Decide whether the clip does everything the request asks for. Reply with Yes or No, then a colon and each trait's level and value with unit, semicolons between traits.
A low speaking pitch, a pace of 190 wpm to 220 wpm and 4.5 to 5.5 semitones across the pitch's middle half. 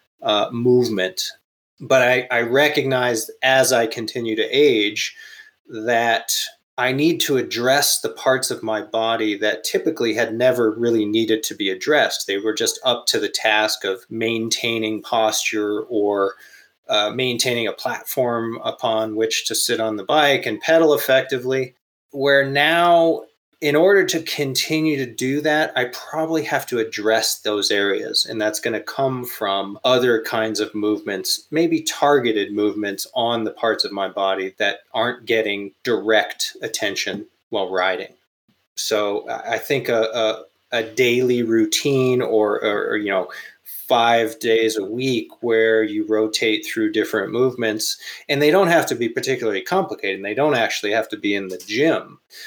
No: low, 115 Hz; average, 160 wpm; average, 4.8 semitones